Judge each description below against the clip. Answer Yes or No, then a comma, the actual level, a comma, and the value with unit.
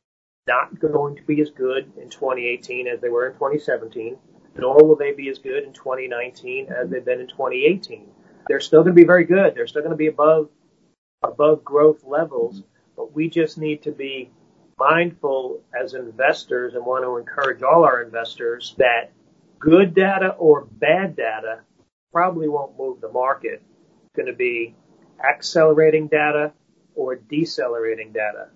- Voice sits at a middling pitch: Yes, medium, 160 Hz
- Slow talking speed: No, average, 165 wpm